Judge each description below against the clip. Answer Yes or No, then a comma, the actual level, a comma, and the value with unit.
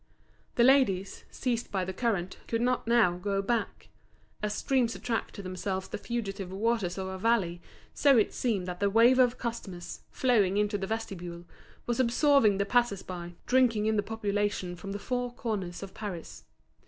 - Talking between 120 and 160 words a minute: No, average, 175 wpm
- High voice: Yes, high, 210 Hz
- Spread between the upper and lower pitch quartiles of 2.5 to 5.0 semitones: Yes, average, 4.0 semitones